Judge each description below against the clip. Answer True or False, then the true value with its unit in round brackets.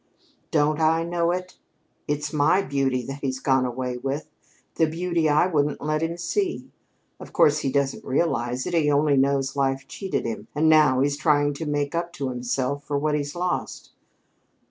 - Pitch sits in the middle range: True (145 Hz)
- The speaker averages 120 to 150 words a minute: False (180 wpm)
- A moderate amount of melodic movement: True (3.0 semitones)